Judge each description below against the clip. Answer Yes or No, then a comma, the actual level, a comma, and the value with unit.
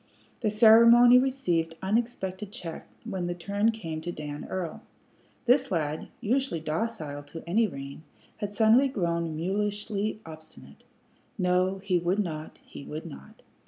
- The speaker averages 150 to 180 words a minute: No, slow, 135 wpm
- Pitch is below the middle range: No, medium, 185 Hz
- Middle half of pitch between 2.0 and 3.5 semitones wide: No, average, 5.2 semitones